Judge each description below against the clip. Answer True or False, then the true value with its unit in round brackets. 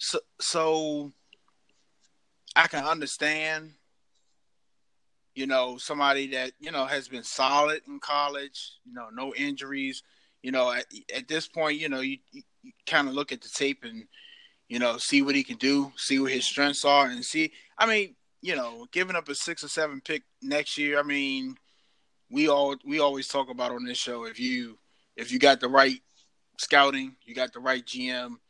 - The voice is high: False (140 Hz)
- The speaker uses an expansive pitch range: False (3.0 semitones)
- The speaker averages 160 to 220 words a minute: True (185 wpm)